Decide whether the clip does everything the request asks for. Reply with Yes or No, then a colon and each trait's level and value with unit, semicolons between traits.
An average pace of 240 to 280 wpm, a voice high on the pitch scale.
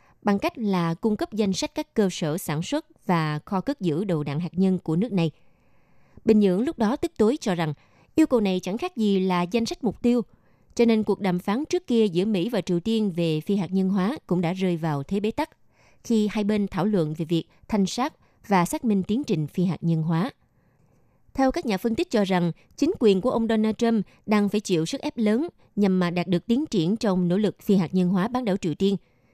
Yes: average, 245 wpm; high, 200 Hz